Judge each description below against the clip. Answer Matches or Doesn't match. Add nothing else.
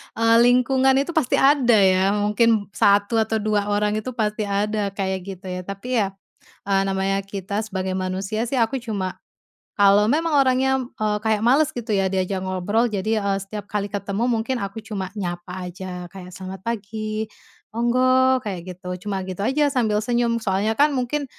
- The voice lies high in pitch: Matches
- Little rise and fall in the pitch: Doesn't match